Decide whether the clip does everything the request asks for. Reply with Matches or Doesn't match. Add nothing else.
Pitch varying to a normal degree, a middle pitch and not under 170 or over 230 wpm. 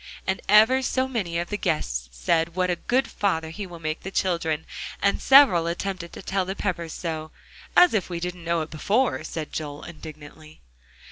Matches